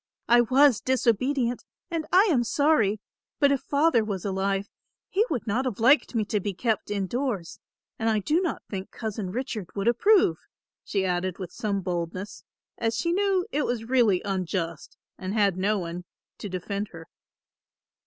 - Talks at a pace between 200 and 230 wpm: No, average, 170 wpm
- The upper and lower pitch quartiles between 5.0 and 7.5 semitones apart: Yes, average, 5.3 semitones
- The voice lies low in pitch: No, high, 215 Hz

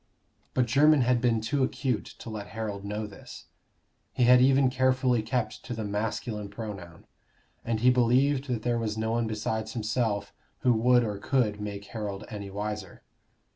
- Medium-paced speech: Yes, average, 170 wpm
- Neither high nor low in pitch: No, low, 115 Hz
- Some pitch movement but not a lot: Yes, average, 3.1 semitones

